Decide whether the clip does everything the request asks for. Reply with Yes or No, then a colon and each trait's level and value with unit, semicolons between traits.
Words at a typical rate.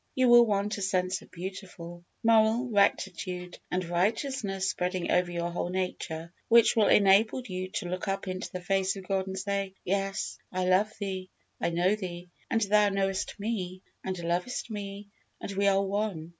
Yes: average, 175 wpm